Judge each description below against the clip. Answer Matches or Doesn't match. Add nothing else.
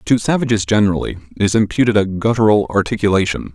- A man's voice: Matches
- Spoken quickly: Doesn't match